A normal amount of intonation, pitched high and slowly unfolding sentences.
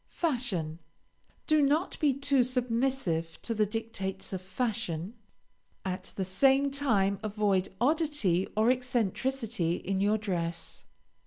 No: wide, 5.9 semitones; high, 220 Hz; slow, 115 wpm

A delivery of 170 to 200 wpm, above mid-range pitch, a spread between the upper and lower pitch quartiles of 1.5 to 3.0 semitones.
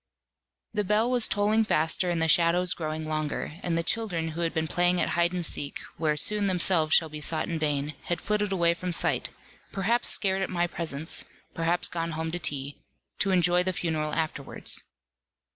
No: average, 190 wpm; medium, 170 Hz; narrow, 2.6 semitones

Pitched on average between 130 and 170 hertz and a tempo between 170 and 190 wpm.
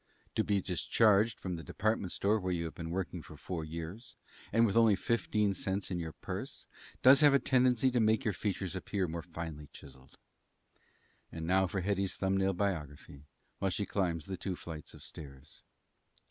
No: very low, 95 Hz; average, 180 wpm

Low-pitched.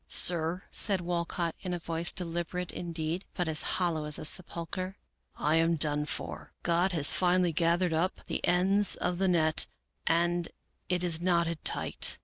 No: medium, 170 Hz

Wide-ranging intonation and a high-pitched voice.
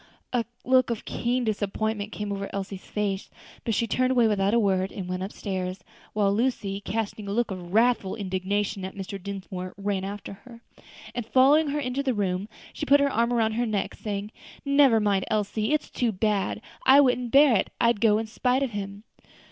No: average, 3.5 semitones; high, 210 Hz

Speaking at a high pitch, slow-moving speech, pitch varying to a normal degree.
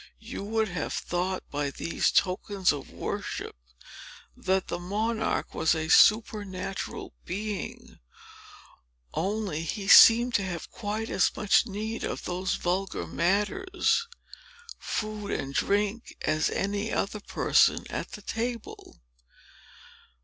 Yes: high, 200 Hz; slow, 115 wpm; average, 3.0 semitones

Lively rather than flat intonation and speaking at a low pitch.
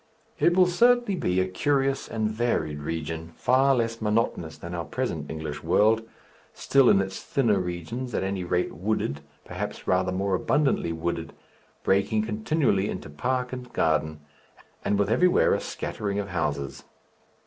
Yes: wide, 6.4 semitones; low, 100 Hz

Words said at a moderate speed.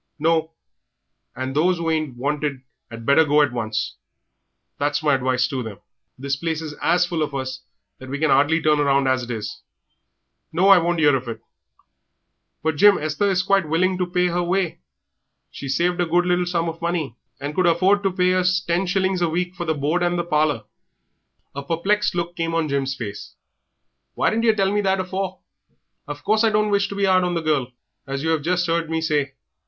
No: fast, 210 wpm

